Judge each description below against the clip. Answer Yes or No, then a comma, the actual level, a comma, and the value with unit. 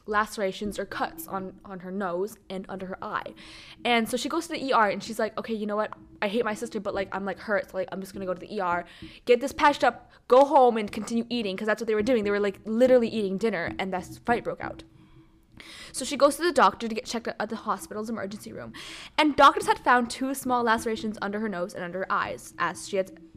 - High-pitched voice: Yes, high, 215 Hz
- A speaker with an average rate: No, fast, 260 wpm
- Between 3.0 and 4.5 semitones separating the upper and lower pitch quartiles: Yes, average, 3.8 semitones